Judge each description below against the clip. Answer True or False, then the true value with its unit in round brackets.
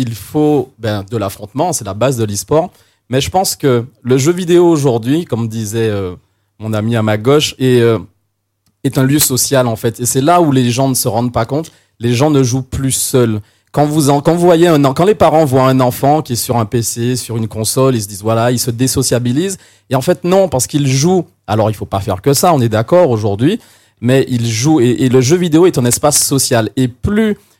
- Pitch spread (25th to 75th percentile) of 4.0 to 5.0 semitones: True (4.5 semitones)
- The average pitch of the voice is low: True (125 Hz)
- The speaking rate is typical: False (230 wpm)